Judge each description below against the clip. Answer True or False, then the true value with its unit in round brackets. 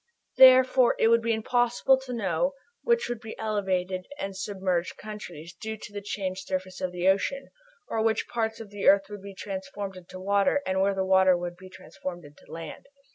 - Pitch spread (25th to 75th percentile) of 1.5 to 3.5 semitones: True (3.1 semitones)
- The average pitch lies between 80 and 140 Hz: False (195 Hz)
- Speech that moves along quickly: False (190 wpm)